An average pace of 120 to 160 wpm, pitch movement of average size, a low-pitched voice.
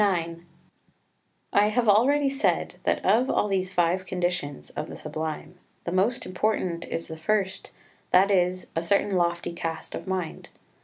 No: average, 155 wpm; average, 3.4 semitones; medium, 185 Hz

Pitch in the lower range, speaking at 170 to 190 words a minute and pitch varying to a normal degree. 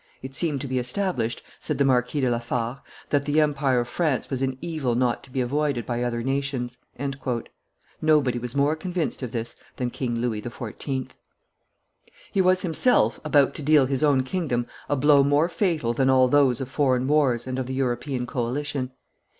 Yes: low, 130 Hz; average, 185 wpm; average, 3.0 semitones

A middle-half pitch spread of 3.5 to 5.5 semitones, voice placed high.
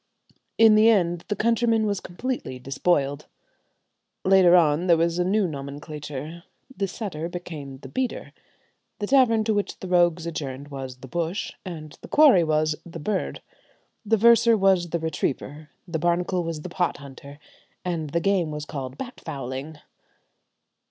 No: average, 4.9 semitones; medium, 170 Hz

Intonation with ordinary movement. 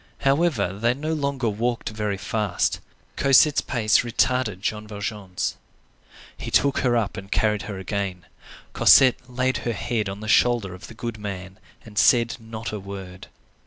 Yes: average, 3.5 semitones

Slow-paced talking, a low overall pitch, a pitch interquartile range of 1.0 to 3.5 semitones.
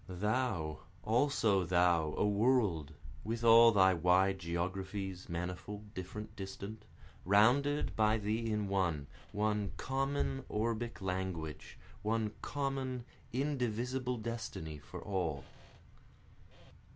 No: slow, 100 wpm; low, 105 Hz; average, 4.2 semitones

